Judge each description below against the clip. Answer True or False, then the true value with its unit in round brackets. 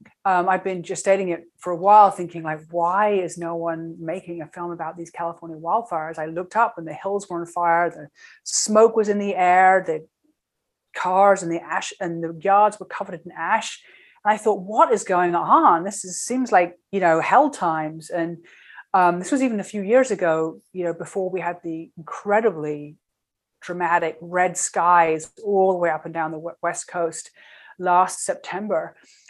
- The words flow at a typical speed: True (195 wpm)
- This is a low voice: False (175 Hz)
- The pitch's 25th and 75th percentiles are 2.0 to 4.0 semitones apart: True (2.8 semitones)